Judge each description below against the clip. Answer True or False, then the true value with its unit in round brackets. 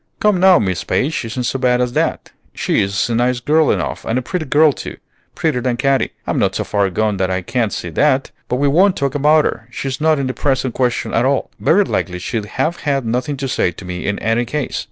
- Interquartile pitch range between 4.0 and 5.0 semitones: True (4.5 semitones)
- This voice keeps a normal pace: False (240 wpm)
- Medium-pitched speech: False (130 Hz)